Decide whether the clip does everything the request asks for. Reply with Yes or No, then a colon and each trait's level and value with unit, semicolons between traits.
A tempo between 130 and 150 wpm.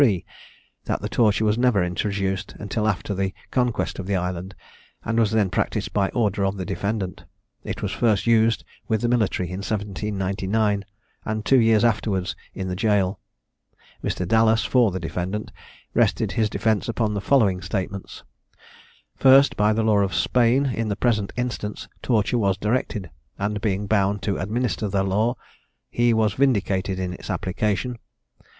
No: average, 160 wpm